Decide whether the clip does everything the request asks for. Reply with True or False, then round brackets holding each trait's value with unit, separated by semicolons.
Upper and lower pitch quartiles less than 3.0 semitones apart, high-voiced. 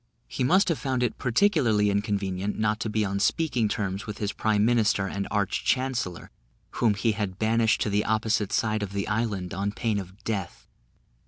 False (2.4 semitones; 105 Hz)